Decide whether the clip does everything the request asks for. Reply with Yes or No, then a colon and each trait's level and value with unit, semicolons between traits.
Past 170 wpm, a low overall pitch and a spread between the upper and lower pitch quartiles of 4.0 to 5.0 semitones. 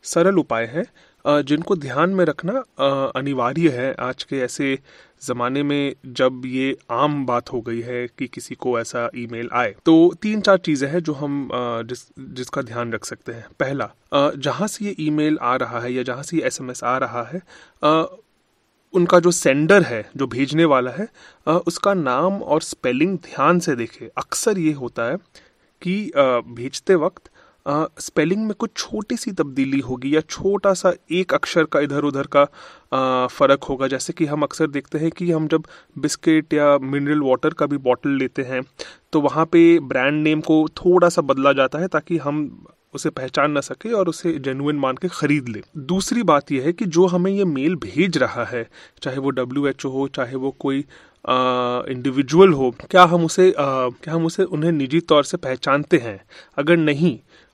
No: average, 185 wpm; medium, 150 Hz; average, 4.6 semitones